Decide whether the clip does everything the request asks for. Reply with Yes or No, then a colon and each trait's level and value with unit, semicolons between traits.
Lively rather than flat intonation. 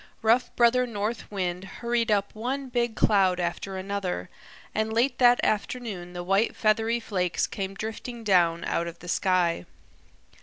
No: average, 4.3 semitones